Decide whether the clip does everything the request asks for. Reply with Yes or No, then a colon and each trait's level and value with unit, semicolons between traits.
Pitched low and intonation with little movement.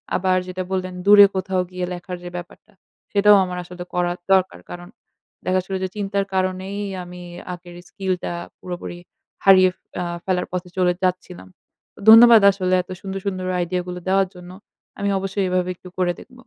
No: medium, 185 Hz; narrow, 1.4 semitones